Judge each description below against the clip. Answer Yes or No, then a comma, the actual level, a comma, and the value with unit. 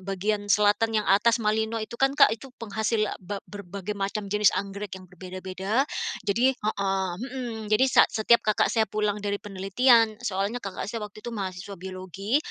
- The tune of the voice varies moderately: No, narrow, 2.1 semitones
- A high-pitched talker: Yes, high, 210 Hz